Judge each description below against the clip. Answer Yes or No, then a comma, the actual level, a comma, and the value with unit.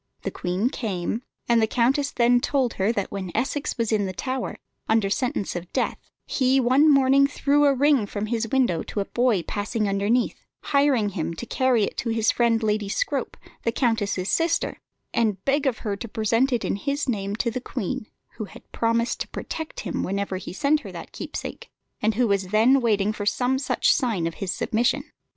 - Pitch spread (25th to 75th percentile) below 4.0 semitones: No, average, 4.3 semitones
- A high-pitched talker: Yes, high, 230 Hz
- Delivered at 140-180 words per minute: No, average, 200 wpm